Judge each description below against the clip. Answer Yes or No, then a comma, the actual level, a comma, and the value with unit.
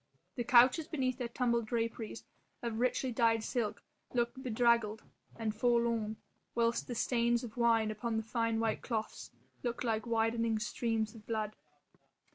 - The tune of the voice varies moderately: No, narrow, 1.4 semitones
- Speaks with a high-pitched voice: Yes, high, 230 Hz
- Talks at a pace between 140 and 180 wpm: Yes, average, 145 wpm